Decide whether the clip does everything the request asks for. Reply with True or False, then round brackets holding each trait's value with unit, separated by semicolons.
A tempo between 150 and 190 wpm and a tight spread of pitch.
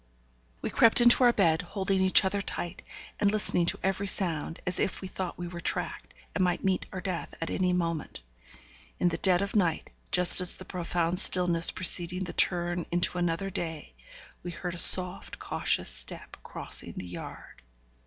True (180 wpm; 1.9 semitones)